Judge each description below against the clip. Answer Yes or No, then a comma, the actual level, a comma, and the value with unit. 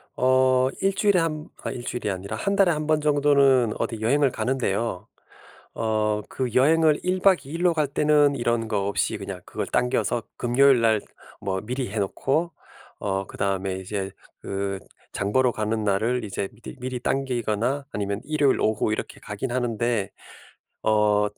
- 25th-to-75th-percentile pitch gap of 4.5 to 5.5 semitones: Yes, average, 5.2 semitones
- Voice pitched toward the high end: No, low, 120 Hz